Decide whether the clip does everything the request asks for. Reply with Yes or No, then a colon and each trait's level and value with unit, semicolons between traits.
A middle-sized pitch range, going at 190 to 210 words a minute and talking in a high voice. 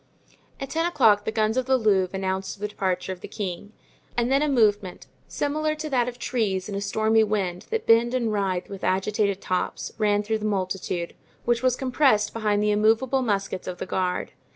Yes: average, 4.1 semitones; average, 200 wpm; high, 210 Hz